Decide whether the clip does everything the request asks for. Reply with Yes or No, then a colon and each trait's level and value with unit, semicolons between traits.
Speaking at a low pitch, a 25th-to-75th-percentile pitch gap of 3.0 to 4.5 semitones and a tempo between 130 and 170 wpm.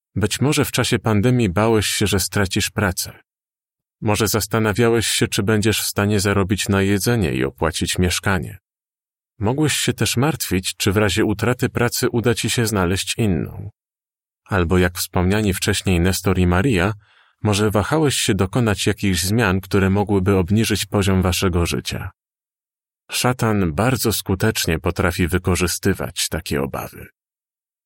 Yes: low, 100 Hz; average, 3.5 semitones; average, 135 wpm